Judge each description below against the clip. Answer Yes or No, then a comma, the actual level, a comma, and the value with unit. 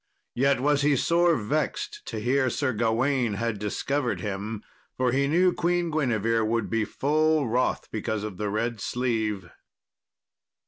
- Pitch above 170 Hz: No, low, 120 Hz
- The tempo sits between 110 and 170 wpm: Yes, average, 145 wpm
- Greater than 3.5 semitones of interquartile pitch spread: Yes, average, 4.6 semitones